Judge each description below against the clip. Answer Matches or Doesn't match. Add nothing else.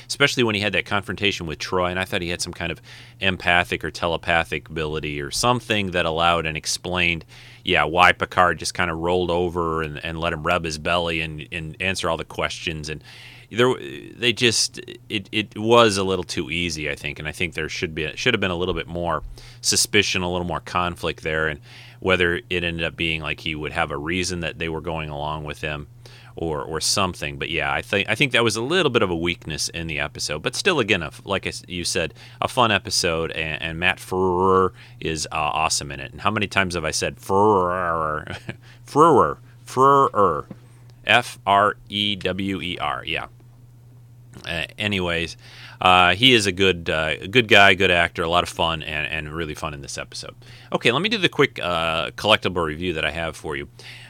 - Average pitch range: Doesn't match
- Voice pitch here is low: Matches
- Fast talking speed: Matches